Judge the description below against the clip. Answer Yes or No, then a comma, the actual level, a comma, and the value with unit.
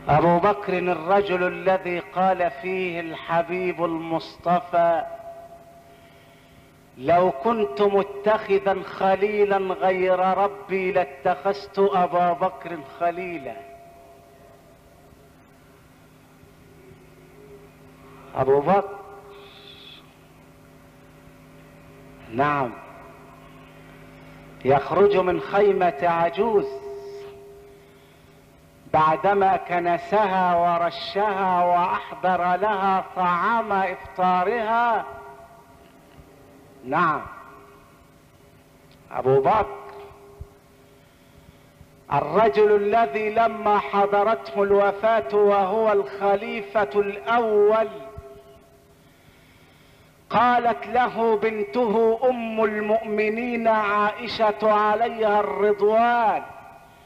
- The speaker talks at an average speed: No, slow, 55 wpm